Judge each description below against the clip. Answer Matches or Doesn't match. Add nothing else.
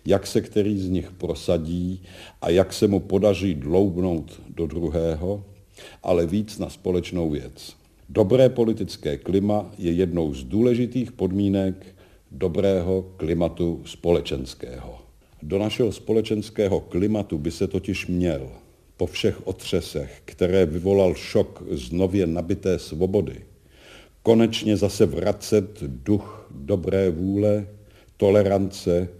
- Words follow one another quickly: Doesn't match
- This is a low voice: Matches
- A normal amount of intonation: Matches